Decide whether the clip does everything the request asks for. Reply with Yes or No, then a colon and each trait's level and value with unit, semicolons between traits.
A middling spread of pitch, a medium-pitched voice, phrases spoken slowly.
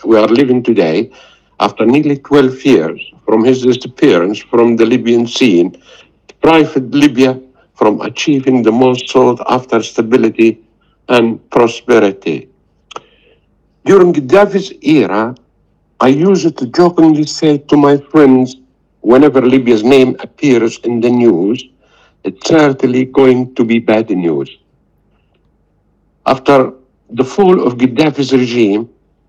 No: average, 3.4 semitones; low, 130 Hz; slow, 115 wpm